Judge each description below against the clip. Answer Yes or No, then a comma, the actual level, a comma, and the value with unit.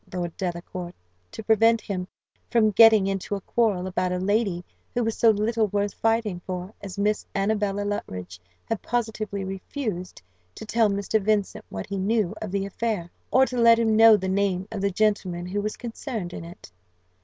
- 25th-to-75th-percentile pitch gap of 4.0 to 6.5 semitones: No, average, 3.1 semitones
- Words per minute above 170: Yes, average, 180 wpm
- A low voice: No, high, 205 Hz